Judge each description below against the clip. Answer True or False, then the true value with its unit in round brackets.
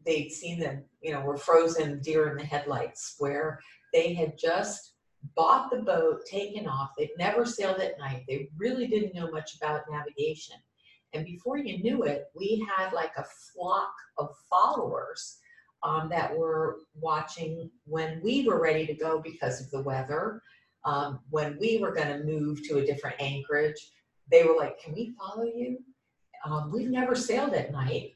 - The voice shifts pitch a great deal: True (7.2 semitones)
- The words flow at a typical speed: True (175 wpm)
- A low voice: False (160 Hz)